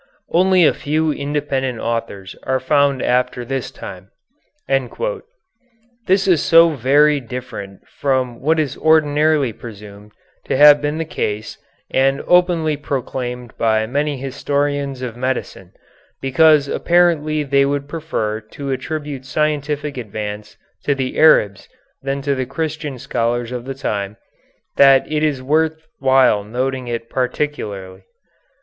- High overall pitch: No, low, 135 Hz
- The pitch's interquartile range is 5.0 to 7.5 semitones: No, average, 3.8 semitones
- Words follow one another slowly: Yes, slow, 130 wpm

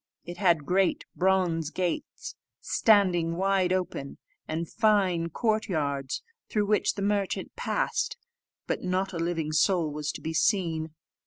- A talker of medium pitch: Yes, medium, 180 Hz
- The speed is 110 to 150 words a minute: Yes, average, 140 wpm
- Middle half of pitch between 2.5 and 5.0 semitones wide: Yes, average, 3.3 semitones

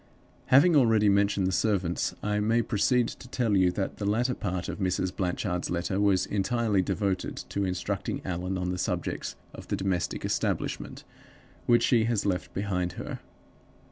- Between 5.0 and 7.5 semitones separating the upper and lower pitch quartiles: No, average, 3.3 semitones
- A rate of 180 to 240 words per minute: No, average, 165 wpm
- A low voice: Yes, low, 100 Hz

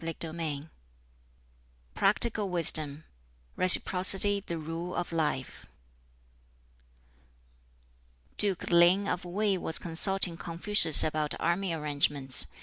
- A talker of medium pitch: Yes, medium, 170 Hz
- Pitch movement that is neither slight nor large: Yes, average, 3.4 semitones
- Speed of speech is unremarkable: No, slow, 95 wpm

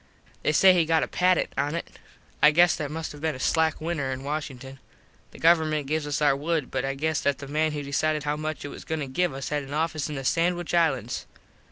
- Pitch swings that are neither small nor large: No, narrow, 2.3 semitones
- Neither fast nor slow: No, fast, 245 wpm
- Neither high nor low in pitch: Yes, medium, 150 Hz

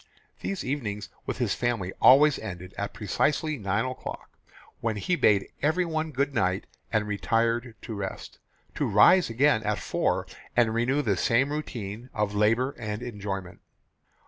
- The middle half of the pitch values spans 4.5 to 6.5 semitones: Yes, average, 4.8 semitones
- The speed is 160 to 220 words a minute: No, average, 145 wpm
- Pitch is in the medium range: No, low, 115 Hz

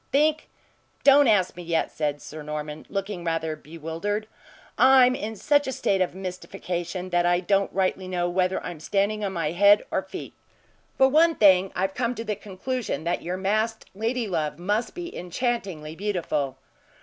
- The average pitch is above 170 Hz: Yes, high, 190 Hz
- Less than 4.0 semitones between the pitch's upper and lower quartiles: No, average, 4.3 semitones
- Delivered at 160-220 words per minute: Yes, average, 170 wpm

